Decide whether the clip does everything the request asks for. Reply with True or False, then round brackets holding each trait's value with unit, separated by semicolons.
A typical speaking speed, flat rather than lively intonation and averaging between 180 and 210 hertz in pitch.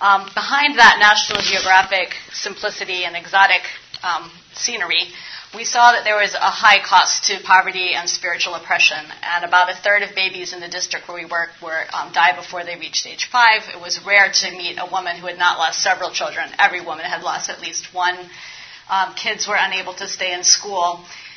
True (195 wpm; 2.3 semitones; 185 Hz)